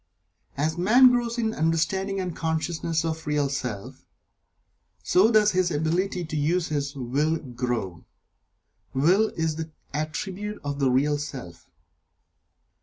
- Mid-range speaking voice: Yes, medium, 160 Hz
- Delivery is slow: Yes, slow, 130 wpm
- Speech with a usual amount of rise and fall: Yes, average, 4.4 semitones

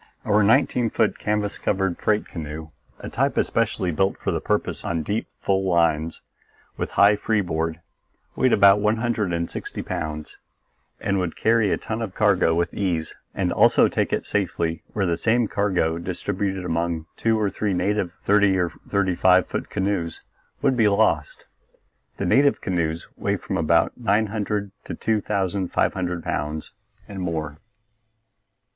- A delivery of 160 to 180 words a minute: Yes, average, 165 wpm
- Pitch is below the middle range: Yes, very low, 95 Hz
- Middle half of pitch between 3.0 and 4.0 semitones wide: Yes, average, 3.7 semitones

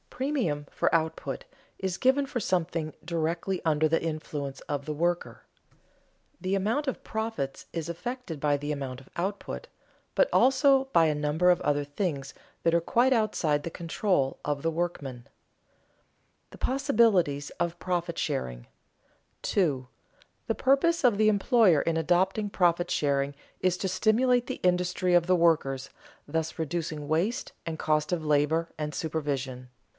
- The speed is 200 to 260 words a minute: No, average, 150 wpm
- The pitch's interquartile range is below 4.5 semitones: No, average, 5.0 semitones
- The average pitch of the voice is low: No, medium, 170 Hz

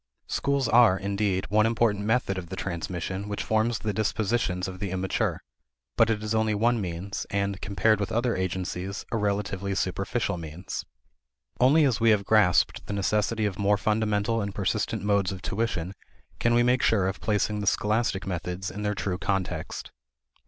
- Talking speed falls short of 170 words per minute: No, average, 175 wpm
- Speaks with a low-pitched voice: Yes, low, 100 Hz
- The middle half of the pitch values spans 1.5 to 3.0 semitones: Yes, narrow, 2.6 semitones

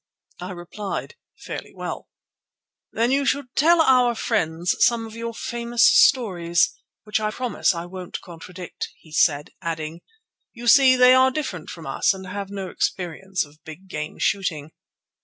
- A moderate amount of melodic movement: No, wide, 5.8 semitones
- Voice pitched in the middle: No, high, 195 Hz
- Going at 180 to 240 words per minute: No, average, 155 wpm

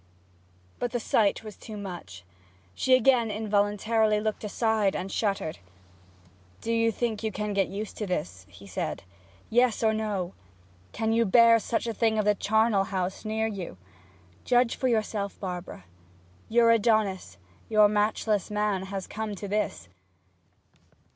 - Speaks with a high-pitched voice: Yes, high, 215 Hz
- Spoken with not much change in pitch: Yes, narrow, 2.3 semitones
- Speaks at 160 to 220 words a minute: No, average, 150 wpm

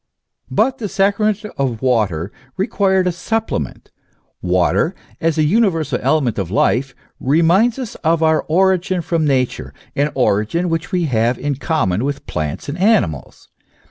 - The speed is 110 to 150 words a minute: Yes, average, 140 wpm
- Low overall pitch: No, medium, 155 Hz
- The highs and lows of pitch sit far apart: Yes, wide, 7.4 semitones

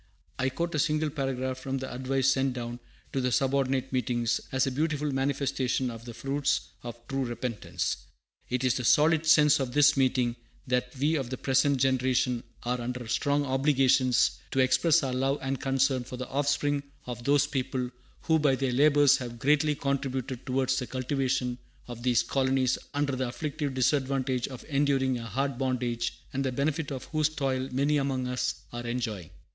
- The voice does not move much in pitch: Yes, narrow, 1.9 semitones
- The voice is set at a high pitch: No, low, 130 Hz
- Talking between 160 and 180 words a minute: Yes, average, 175 wpm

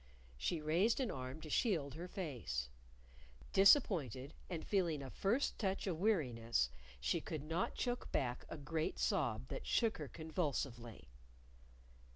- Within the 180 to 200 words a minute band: No, average, 140 wpm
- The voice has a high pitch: No, medium, 155 Hz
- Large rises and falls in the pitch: Yes, wide, 6.7 semitones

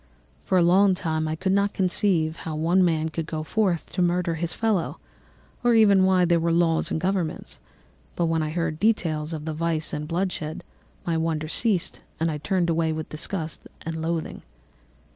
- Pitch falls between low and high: Yes, medium, 165 Hz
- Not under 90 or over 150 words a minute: No, average, 180 wpm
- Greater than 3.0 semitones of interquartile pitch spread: No, average, 2.7 semitones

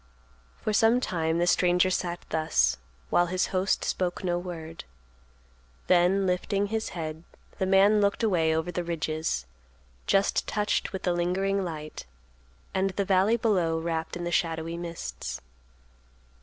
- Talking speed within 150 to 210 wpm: No, average, 140 wpm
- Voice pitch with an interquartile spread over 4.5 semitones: No, average, 2.9 semitones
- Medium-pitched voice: Yes, medium, 175 Hz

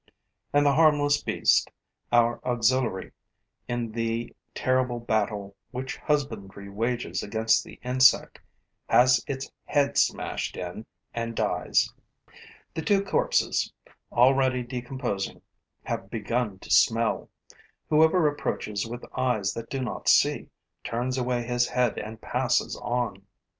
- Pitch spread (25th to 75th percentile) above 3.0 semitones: No, narrow, 2.6 semitones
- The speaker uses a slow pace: Yes, slow, 120 wpm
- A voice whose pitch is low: Yes, low, 120 Hz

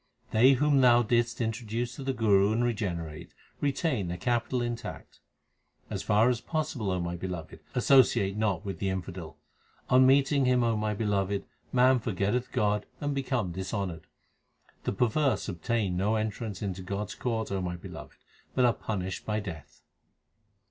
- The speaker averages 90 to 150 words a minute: No, average, 160 wpm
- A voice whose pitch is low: Yes, low, 110 Hz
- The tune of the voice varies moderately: Yes, average, 4.5 semitones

